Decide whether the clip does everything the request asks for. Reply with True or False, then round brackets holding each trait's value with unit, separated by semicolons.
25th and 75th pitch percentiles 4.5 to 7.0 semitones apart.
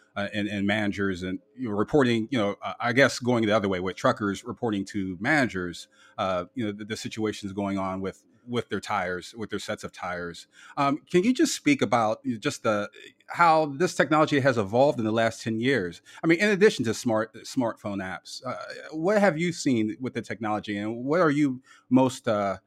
True (5.4 semitones)